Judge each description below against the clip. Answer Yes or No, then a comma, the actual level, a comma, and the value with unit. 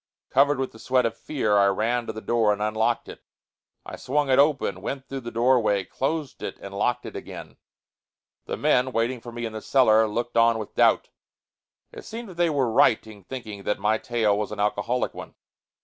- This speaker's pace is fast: Yes, fast, 210 wpm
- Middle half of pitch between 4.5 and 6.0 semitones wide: No, average, 3.5 semitones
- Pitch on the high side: No, low, 115 Hz